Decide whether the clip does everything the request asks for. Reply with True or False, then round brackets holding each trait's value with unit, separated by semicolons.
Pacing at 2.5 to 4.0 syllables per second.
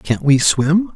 True (3.3 syllables/s)